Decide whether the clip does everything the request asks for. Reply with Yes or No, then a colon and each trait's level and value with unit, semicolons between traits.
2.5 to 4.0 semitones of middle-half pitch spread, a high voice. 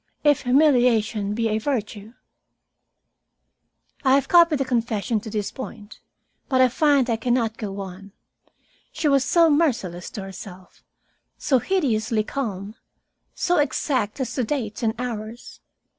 No: average, 4.4 semitones; high, 235 Hz